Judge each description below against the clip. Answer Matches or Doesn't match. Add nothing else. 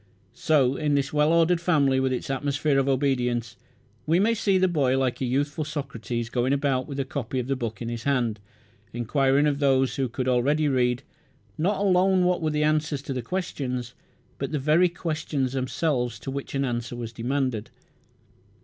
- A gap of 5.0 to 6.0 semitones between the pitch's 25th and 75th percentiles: Doesn't match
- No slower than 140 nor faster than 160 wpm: Doesn't match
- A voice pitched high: Doesn't match